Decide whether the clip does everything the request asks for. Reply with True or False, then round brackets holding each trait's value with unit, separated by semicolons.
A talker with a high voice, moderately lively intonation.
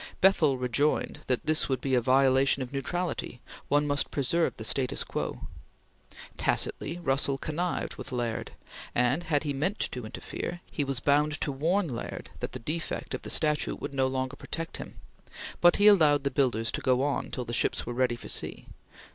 False (140 Hz; 3.3 semitones)